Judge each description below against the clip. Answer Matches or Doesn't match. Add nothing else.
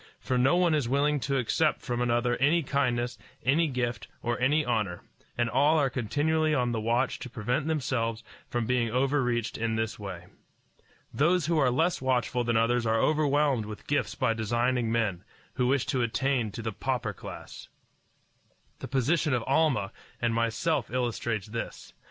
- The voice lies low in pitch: Matches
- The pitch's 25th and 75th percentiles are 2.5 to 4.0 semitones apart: Matches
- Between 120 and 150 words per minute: Doesn't match